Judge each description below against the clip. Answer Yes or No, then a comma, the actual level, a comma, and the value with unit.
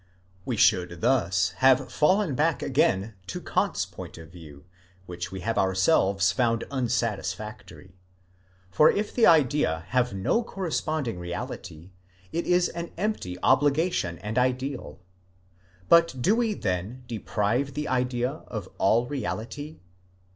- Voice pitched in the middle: No, low, 120 Hz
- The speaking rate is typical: No, slow, 125 wpm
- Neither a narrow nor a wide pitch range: No, wide, 7.6 semitones